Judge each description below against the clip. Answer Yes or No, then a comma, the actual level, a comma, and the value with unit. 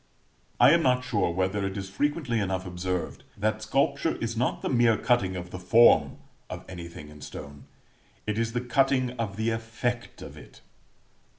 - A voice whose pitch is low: Yes, low, 110 Hz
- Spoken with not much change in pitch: No, average, 4.7 semitones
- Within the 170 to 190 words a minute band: Yes, average, 175 wpm